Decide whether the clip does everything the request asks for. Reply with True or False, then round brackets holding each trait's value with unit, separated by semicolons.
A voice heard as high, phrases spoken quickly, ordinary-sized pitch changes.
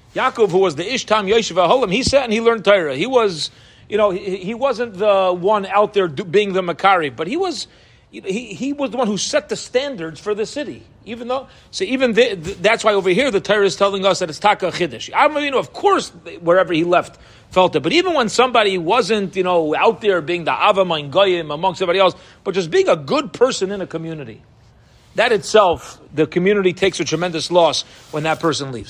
True (195 Hz; 220 wpm; 4.6 semitones)